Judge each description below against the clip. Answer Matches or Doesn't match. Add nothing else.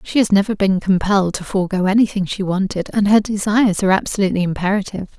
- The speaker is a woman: Matches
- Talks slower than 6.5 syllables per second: Doesn't match